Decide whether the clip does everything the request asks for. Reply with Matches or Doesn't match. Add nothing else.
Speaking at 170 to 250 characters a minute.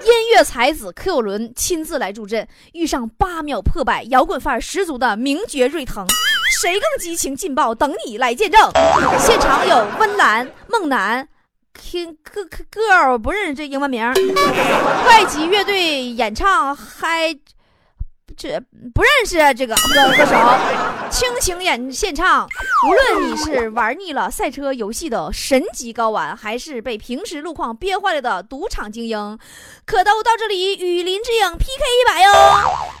Matches